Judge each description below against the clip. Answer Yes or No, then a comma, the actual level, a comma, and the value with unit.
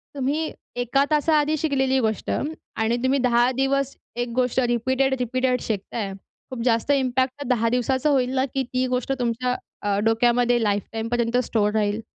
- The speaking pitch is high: Yes, very high, 250 Hz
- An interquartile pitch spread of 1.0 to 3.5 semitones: Yes, narrow, 2.4 semitones